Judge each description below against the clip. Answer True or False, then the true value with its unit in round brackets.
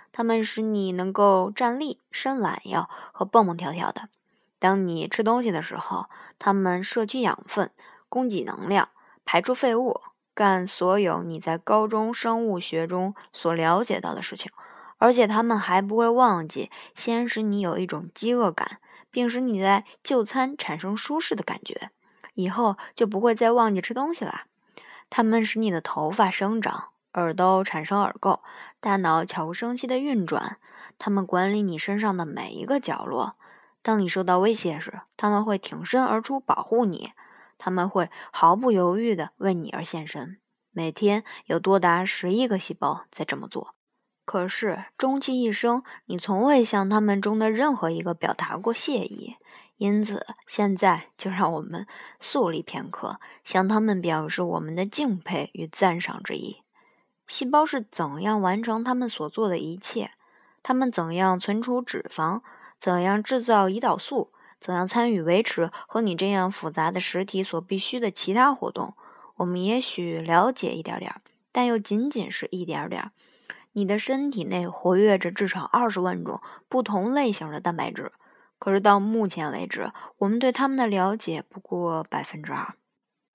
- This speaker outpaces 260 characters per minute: False (245 characters per minute)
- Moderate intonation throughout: True (4.5 semitones)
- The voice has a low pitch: False (205 Hz)